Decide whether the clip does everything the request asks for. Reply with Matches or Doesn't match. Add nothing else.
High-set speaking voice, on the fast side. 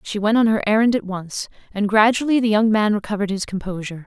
Matches